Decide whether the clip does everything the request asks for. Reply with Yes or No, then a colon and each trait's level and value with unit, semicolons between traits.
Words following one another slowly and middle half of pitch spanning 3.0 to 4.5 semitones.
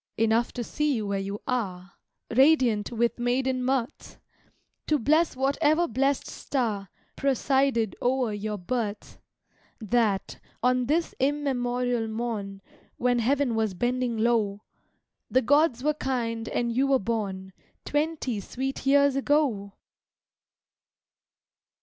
Yes: slow, 115 wpm; average, 3.7 semitones